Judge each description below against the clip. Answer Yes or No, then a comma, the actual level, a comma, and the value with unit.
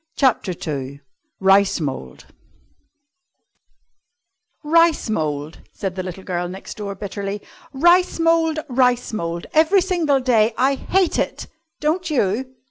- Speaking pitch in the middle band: No, high, 225 Hz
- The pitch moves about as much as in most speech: No, wide, 8.9 semitones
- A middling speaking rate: No, slow, 120 wpm